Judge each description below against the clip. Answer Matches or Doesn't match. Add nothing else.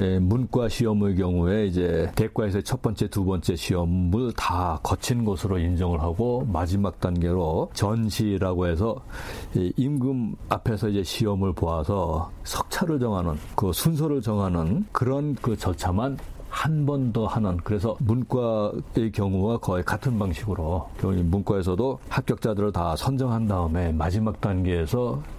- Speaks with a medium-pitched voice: Doesn't match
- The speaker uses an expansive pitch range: Doesn't match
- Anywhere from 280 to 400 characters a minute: Matches